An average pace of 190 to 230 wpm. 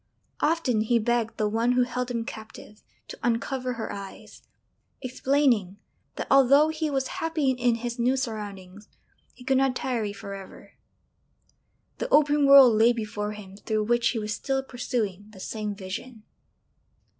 No: average, 155 wpm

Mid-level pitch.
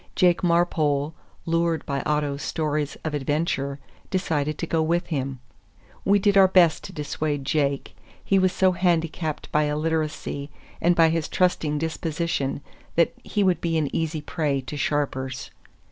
Yes: medium, 155 Hz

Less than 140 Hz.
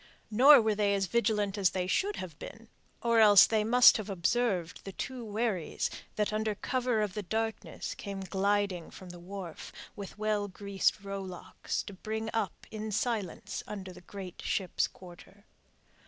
No: high, 205 Hz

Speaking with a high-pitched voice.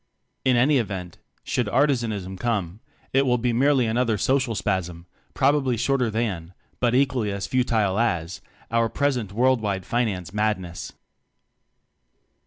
No: low, 115 Hz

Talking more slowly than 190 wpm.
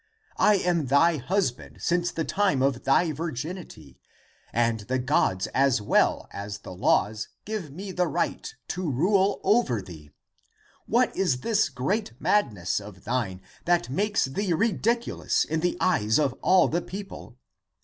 Yes: average, 150 wpm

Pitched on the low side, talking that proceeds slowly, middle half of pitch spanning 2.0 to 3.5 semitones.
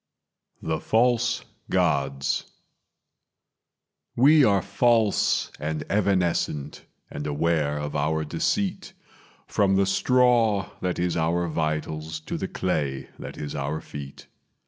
No: very low, 85 Hz; slow, 110 wpm; average, 5.0 semitones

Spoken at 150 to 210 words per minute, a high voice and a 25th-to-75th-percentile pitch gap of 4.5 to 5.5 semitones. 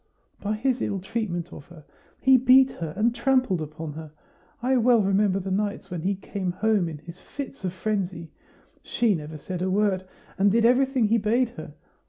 Yes: average, 190 wpm; high, 200 Hz; average, 5.0 semitones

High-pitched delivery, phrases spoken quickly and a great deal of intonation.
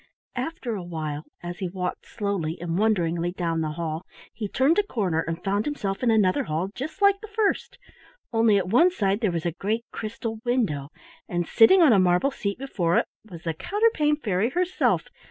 No: high, 200 Hz; average, 190 wpm; wide, 6.4 semitones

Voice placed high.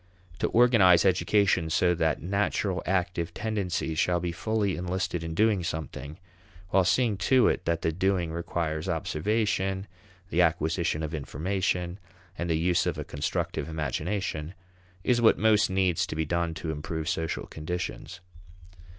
No: very low, 90 Hz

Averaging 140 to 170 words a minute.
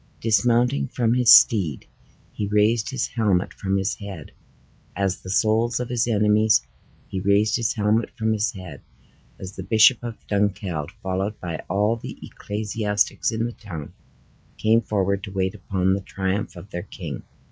Yes: average, 160 wpm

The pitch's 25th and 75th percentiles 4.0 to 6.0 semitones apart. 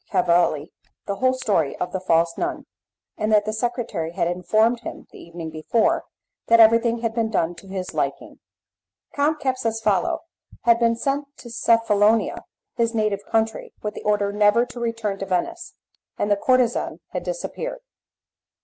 No: average, 3.3 semitones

